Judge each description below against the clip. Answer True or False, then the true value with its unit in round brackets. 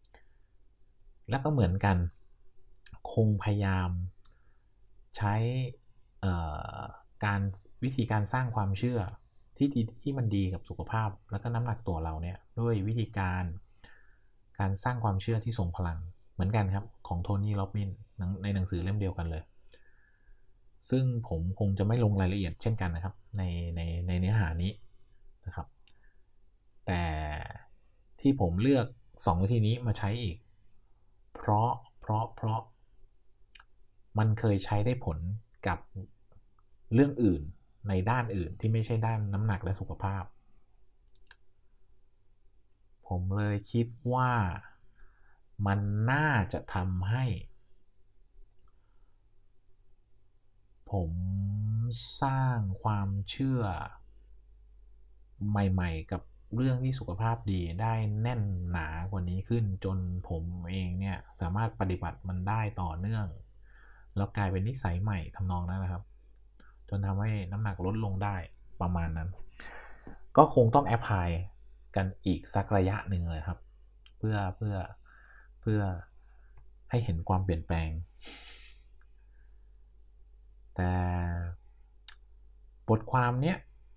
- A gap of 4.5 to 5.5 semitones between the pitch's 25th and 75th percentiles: False (2.6 semitones)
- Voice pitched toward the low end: True (100 Hz)